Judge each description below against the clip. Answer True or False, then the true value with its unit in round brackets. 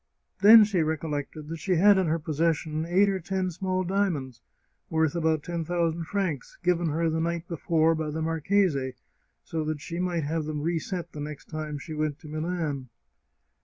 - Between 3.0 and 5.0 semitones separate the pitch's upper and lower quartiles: False (2.4 semitones)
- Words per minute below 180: False (185 wpm)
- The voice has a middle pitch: True (165 Hz)